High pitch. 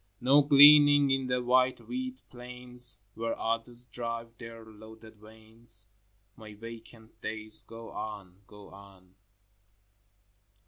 No: low, 115 Hz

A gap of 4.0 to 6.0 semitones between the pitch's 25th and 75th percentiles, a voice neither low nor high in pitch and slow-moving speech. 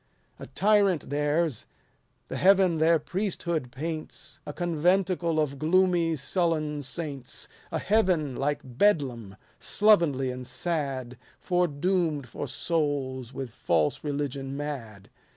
Yes: average, 4.4 semitones; medium, 150 Hz; slow, 110 wpm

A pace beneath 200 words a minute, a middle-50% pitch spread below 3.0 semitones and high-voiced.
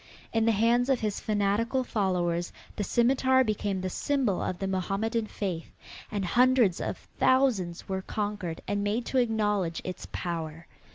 No: average, 155 wpm; average, 4.0 semitones; high, 205 Hz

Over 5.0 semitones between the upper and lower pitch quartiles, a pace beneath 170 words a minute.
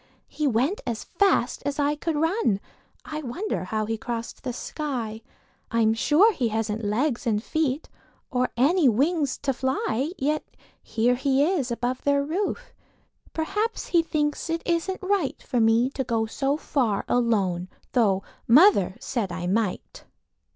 Yes: wide, 5.5 semitones; average, 150 wpm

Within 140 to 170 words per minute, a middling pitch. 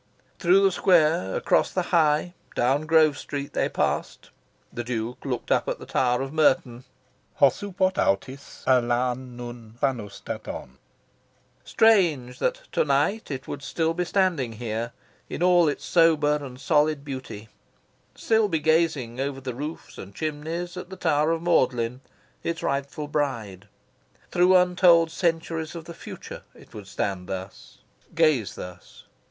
Yes: average, 145 wpm; medium, 145 Hz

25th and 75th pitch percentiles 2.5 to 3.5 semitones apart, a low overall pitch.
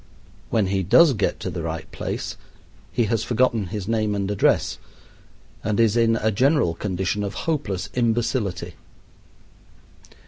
Yes: average, 3.2 semitones; low, 110 Hz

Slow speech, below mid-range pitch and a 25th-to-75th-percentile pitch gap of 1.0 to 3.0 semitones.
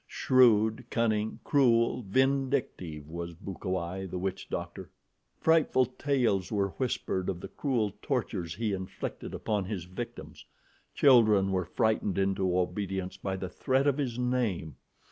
No: slow, 130 wpm; low, 105 Hz; average, 5.1 semitones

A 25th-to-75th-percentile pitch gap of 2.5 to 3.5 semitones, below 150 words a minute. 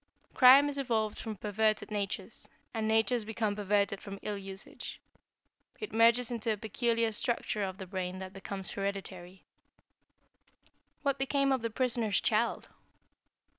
Yes: average, 3.0 semitones; slow, 135 wpm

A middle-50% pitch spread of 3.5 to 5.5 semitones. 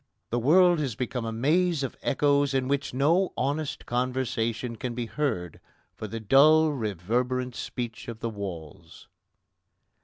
Yes: average, 3.9 semitones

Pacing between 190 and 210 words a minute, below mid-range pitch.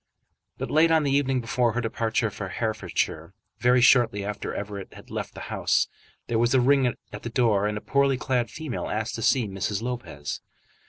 Yes: average, 195 wpm; low, 120 Hz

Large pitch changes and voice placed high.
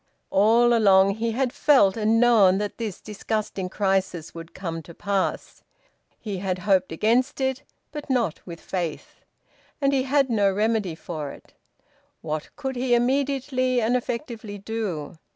No: average, 4.6 semitones; high, 215 Hz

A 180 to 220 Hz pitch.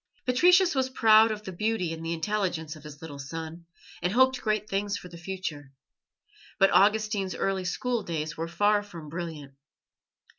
Yes: high, 190 Hz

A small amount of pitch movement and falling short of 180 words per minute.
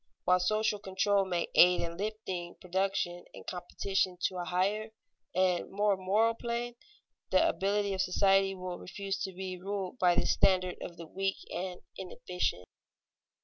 Yes: narrow, 1.9 semitones; average, 150 wpm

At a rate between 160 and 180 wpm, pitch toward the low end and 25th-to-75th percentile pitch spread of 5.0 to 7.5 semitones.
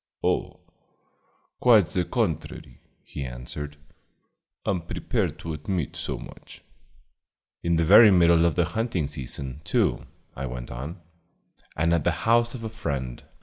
No: average, 140 wpm; very low, 85 Hz; wide, 5.4 semitones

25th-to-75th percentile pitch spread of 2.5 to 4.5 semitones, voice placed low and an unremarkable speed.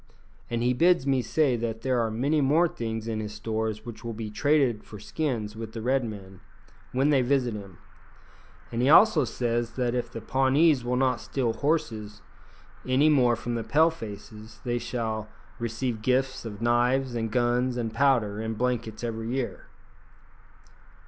Yes: average, 3.0 semitones; low, 120 Hz; average, 170 wpm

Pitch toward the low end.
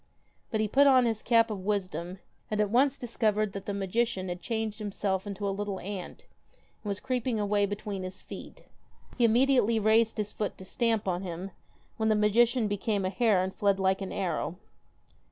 No: high, 210 Hz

